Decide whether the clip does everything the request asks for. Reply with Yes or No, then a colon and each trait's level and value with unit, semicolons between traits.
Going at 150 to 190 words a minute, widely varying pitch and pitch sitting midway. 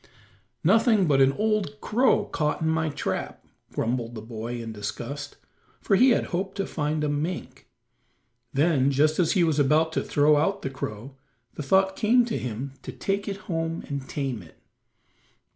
Yes: average, 175 wpm; wide, 6.1 semitones; medium, 150 Hz